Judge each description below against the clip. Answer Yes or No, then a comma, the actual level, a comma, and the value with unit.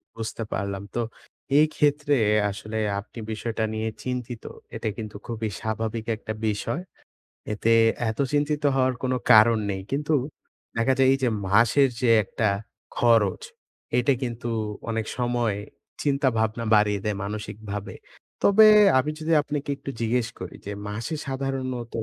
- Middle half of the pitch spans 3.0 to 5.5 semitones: Yes, average, 3.5 semitones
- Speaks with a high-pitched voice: No, low, 115 Hz